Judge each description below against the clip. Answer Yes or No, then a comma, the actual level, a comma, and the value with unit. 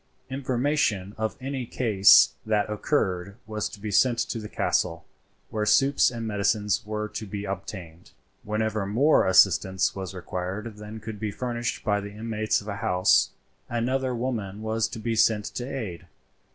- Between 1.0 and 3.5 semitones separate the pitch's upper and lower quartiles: Yes, average, 2.8 semitones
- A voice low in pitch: Yes, low, 105 Hz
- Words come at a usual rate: Yes, average, 160 wpm